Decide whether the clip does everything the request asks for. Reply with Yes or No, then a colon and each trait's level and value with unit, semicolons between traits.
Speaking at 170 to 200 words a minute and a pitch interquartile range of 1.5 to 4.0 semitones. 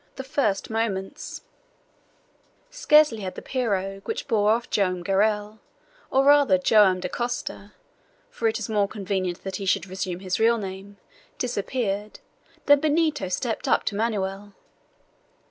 No: slow, 135 wpm; average, 3.4 semitones